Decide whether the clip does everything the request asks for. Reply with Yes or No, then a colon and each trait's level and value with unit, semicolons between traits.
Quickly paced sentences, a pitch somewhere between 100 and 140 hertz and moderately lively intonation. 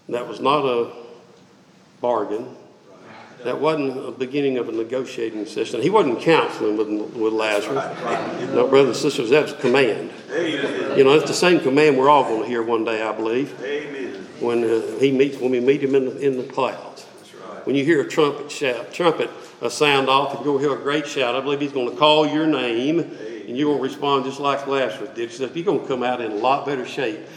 Yes: fast, 215 wpm; low, 135 Hz; average, 3.2 semitones